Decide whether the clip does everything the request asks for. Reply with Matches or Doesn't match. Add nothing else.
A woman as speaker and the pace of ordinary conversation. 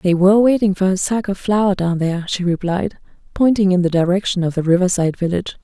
Doesn't match